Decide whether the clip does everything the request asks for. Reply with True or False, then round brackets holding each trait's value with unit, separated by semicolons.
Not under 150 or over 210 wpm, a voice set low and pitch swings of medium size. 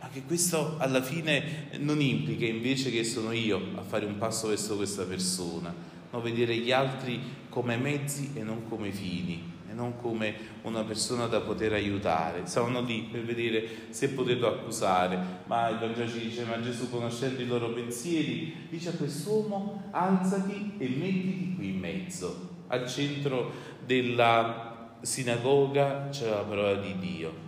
True (155 wpm; 120 Hz; 4.5 semitones)